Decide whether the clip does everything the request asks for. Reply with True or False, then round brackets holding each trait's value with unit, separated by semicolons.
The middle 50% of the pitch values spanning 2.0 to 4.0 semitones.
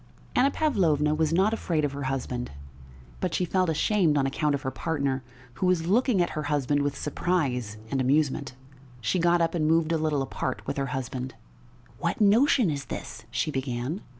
False (4.4 semitones)